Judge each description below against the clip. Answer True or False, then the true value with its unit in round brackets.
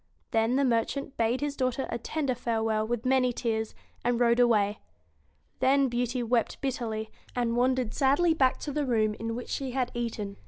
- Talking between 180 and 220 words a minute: True (185 wpm)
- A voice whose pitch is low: False (240 Hz)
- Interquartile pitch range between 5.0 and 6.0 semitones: False (2.6 semitones)